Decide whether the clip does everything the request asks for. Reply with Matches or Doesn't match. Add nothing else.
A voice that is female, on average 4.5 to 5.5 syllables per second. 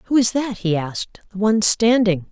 Matches